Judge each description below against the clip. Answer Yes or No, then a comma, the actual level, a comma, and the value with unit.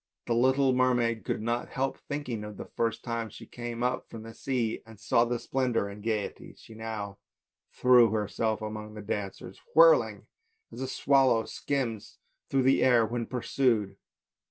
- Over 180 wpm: No, average, 175 wpm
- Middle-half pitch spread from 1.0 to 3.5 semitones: Yes, average, 2.8 semitones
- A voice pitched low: Yes, low, 115 Hz